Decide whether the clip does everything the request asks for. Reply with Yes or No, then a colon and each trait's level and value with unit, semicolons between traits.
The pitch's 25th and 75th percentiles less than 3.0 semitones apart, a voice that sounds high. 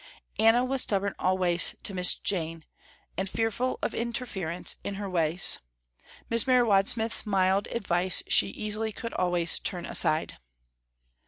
No: average, 4.0 semitones; high, 195 Hz